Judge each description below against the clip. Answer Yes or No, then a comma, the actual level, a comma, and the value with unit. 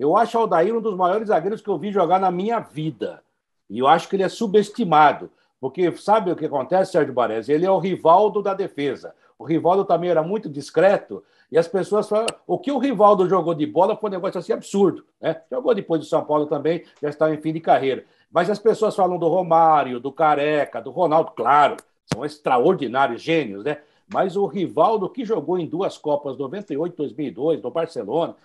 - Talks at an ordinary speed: No, fast, 210 wpm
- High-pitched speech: No, medium, 170 Hz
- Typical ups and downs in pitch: Yes, average, 4.7 semitones